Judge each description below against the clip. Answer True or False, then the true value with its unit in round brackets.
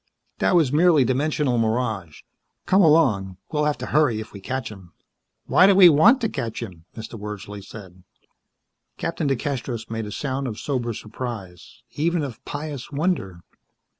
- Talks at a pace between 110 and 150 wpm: False (160 wpm)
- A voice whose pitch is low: True (125 Hz)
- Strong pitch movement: True (6.1 semitones)